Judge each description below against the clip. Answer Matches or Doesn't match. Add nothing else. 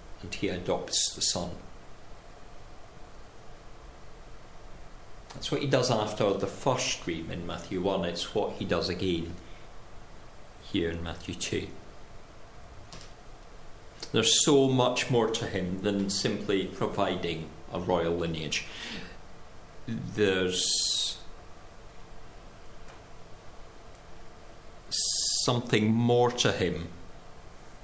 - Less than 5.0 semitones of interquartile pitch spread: Matches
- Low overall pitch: Matches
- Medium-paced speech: Doesn't match